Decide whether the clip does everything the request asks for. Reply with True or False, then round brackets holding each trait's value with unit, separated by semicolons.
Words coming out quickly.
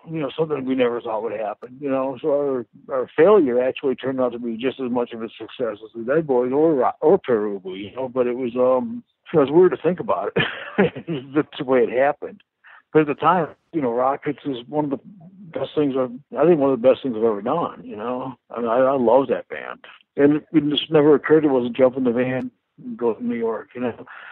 True (255 wpm)